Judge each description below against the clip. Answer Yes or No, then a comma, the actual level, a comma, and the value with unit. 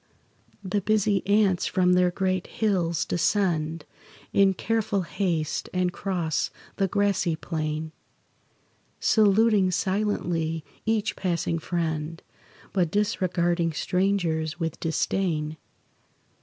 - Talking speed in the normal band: No, slow, 95 wpm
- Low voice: No, medium, 180 Hz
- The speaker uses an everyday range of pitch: Yes, average, 3.4 semitones